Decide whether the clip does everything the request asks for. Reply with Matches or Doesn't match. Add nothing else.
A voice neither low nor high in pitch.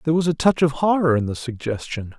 Matches